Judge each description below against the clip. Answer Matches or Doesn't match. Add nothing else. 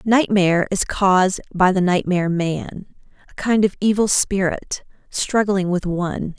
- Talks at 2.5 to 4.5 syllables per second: Matches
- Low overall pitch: Doesn't match